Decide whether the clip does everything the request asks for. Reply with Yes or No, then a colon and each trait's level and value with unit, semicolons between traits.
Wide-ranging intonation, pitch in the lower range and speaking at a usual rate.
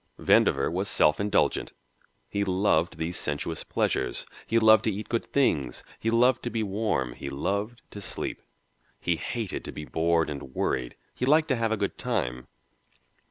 Yes: wide, 6.5 semitones; low, 100 Hz; average, 170 wpm